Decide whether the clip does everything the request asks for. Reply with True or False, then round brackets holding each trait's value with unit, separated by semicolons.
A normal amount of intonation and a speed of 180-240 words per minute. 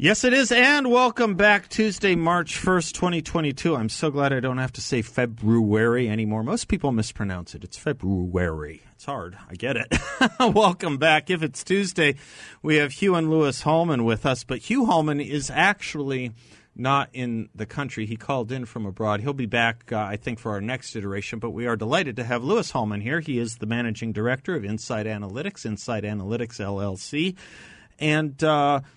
False (6.5 semitones; 185 wpm)